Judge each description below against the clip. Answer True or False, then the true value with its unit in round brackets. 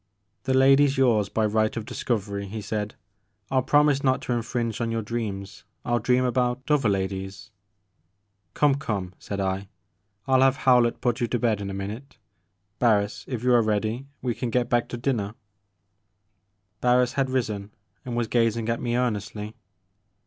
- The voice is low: True (115 Hz)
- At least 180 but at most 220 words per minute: True (190 wpm)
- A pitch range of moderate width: True (3.6 semitones)